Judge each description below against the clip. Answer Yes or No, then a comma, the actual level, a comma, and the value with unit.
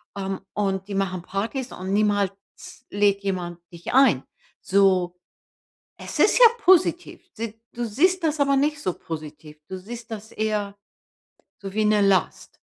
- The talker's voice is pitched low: No, high, 205 Hz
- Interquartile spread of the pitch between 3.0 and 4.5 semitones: Yes, average, 3.9 semitones